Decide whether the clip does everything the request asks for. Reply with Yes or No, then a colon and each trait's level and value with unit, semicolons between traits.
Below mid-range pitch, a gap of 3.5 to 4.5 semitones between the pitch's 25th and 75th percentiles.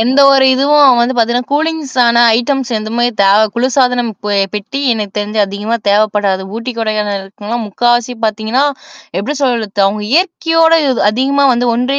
No: high, 240 Hz; average, 4.0 semitones